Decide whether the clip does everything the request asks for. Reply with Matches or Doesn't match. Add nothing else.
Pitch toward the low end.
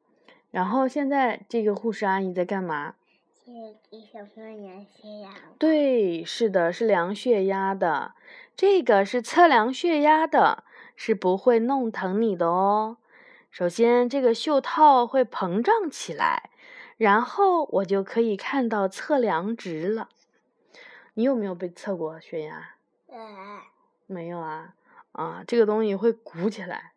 Doesn't match